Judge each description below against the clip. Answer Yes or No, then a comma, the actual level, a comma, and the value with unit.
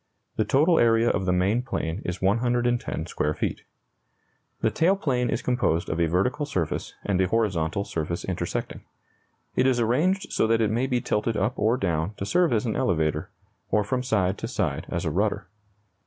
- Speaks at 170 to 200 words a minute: Yes, average, 185 wpm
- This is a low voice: Yes, low, 110 Hz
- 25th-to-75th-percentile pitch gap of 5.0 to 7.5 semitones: Yes, average, 5.3 semitones